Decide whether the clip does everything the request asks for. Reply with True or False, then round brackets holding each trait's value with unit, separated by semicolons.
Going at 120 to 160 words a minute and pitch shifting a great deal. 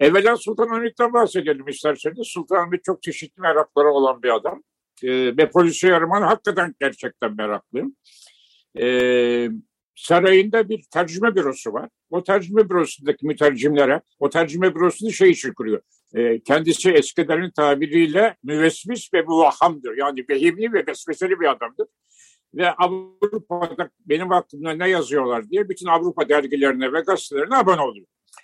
True (135 wpm; 6.8 semitones)